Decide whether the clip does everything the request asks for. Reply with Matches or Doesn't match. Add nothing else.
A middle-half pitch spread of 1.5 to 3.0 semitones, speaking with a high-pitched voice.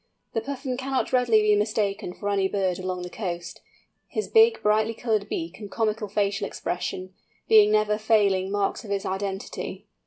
Matches